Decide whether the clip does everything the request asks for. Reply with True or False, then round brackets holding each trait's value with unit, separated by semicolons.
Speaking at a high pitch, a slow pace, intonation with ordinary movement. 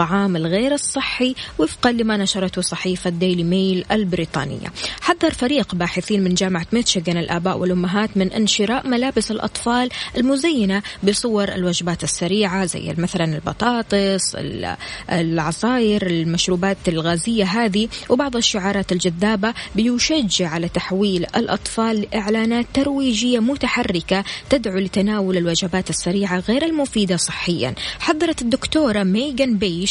False (200 Hz; 110 wpm; 4.7 semitones)